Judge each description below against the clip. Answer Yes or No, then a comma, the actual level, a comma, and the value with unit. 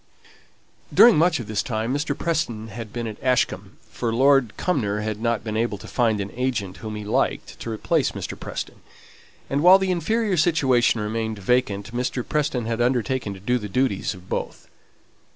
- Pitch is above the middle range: No, low, 115 Hz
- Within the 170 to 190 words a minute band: Yes, average, 180 wpm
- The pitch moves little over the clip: No, average, 3.8 semitones